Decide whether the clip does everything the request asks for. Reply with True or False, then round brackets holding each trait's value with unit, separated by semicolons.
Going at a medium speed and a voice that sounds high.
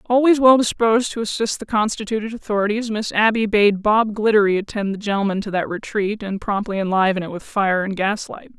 True (190 wpm; 210 Hz)